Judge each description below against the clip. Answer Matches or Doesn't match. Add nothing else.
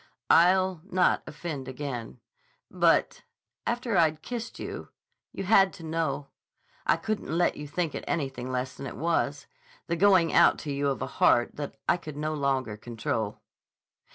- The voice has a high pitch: Doesn't match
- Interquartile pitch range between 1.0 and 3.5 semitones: Doesn't match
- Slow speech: Doesn't match